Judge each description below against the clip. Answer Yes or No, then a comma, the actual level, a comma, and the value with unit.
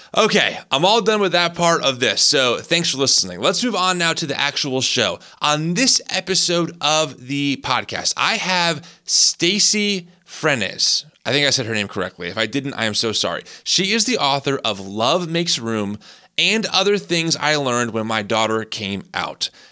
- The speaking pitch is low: No, medium, 150 Hz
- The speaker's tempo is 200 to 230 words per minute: No, average, 190 wpm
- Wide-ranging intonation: Yes, wide, 7.2 semitones